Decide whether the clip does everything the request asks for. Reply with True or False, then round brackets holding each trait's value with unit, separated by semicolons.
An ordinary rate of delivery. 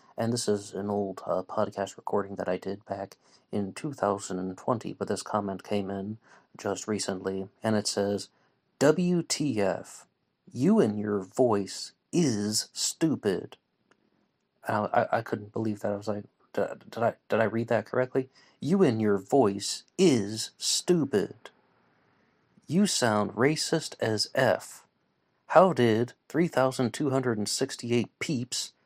False (130 wpm)